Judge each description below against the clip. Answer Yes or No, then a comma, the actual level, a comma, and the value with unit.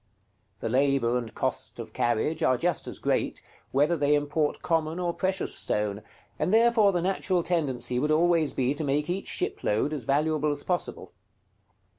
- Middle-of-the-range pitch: Yes, medium, 150 Hz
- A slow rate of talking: No, average, 165 wpm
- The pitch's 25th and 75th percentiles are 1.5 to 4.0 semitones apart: No, average, 4.5 semitones